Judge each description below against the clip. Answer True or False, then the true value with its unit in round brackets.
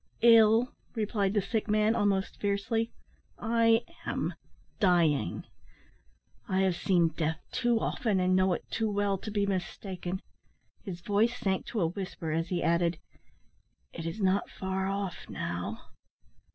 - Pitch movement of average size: True (3.1 semitones)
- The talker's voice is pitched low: False (195 Hz)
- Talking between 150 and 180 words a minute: False (140 wpm)